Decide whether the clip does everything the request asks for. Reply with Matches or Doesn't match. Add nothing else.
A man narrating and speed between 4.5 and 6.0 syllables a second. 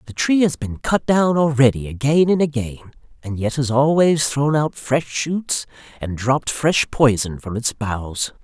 Doesn't match